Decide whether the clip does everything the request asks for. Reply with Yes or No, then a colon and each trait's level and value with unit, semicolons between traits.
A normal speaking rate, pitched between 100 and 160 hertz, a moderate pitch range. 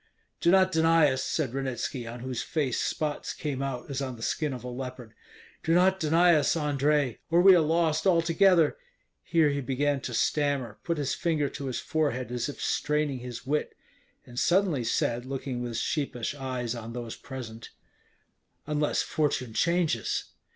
Yes: average, 170 wpm; medium, 140 Hz; average, 4.2 semitones